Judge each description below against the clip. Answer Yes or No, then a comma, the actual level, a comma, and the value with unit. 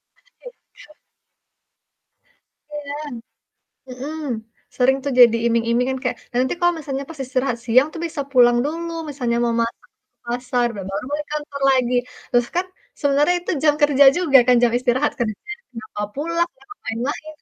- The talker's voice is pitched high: Yes, very high, 265 Hz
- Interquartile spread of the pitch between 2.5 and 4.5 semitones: Yes, average, 3.7 semitones